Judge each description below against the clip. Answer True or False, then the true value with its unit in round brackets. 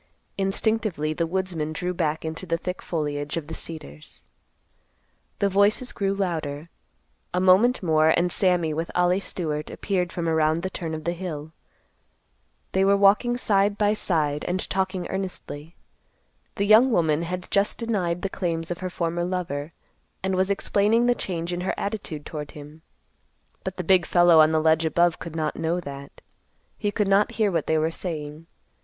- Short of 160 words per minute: False (175 wpm)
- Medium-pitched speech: True (175 Hz)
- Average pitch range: True (3.5 semitones)